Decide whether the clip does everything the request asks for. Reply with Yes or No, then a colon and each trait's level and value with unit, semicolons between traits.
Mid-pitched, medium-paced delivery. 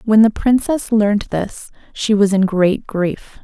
No: high, 205 Hz; average, 175 wpm